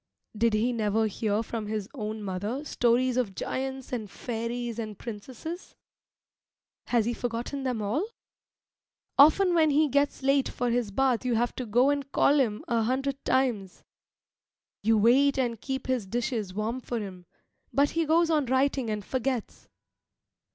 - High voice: Yes, high, 245 Hz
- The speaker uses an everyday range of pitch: Yes, average, 3.7 semitones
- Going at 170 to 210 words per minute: No, average, 160 wpm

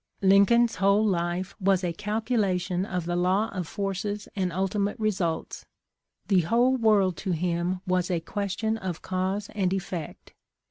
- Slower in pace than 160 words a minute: Yes, average, 150 wpm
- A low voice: No, high, 190 Hz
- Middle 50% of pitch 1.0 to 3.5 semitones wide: Yes, narrow, 2.5 semitones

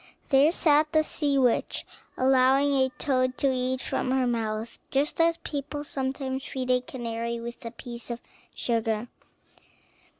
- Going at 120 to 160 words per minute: Yes, average, 145 wpm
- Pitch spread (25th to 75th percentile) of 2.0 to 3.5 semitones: Yes, average, 2.7 semitones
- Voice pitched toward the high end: Yes, very high, 260 Hz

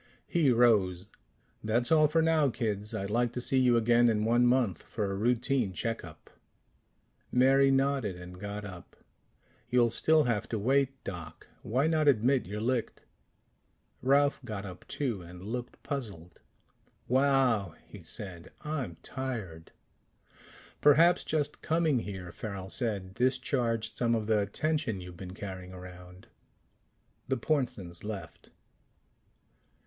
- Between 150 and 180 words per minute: No, slow, 135 wpm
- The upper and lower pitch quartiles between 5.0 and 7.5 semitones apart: Yes, wide, 5.5 semitones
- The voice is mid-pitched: No, low, 115 Hz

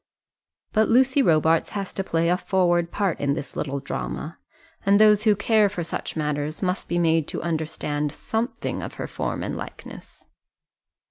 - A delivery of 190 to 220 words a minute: No, average, 170 wpm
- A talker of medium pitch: Yes, medium, 175 Hz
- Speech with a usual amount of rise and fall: Yes, average, 4.8 semitones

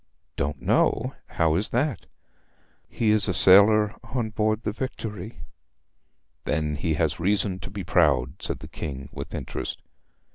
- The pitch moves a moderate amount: No, wide, 5.7 semitones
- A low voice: Yes, very low, 95 Hz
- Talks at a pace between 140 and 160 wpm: Yes, average, 145 wpm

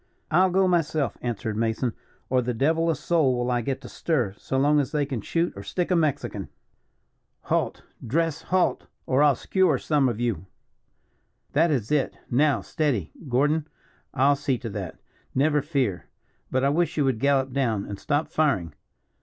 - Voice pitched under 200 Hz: Yes, medium, 140 Hz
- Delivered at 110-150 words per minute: No, average, 175 wpm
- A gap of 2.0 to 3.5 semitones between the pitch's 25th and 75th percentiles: No, average, 4.4 semitones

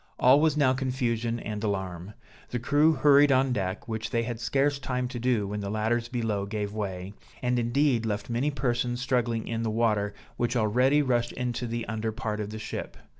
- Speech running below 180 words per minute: No, average, 195 wpm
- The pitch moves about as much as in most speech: Yes, average, 3.0 semitones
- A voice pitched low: Yes, low, 120 Hz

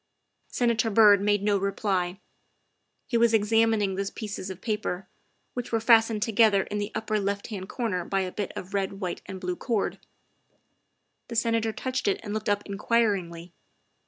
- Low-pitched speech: No, high, 205 Hz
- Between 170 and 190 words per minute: Yes, average, 180 wpm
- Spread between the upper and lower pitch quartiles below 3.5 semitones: Yes, narrow, 2.5 semitones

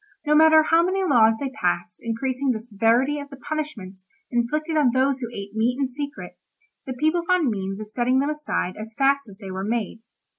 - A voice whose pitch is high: Yes, very high, 255 Hz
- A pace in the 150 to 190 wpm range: No, average, 200 wpm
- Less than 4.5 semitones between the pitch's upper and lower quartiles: No, average, 5.1 semitones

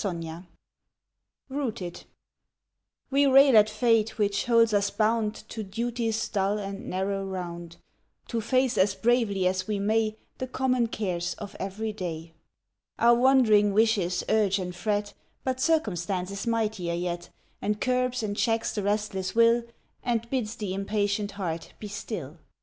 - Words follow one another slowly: No, average, 145 wpm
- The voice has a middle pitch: No, high, 210 Hz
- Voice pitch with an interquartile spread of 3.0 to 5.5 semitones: Yes, average, 3.3 semitones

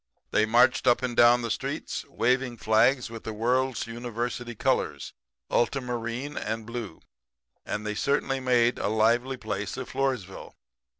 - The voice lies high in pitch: No, low, 120 Hz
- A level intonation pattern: Yes, narrow, 2.3 semitones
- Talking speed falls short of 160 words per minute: Yes, average, 145 wpm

